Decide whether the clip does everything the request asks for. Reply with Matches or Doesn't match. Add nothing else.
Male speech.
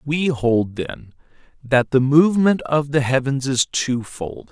Matches